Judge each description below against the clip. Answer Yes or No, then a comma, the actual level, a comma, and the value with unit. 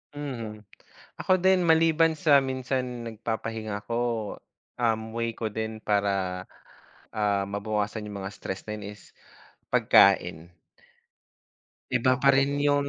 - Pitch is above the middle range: No, low, 115 Hz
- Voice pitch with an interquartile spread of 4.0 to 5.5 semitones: Yes, average, 4.8 semitones